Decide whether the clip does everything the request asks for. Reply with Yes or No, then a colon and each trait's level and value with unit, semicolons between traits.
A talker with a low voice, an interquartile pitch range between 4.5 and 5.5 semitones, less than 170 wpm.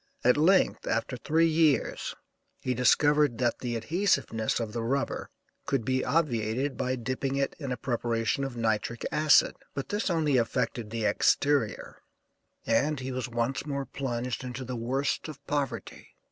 No: low, 130 Hz; average, 3.5 semitones; average, 155 wpm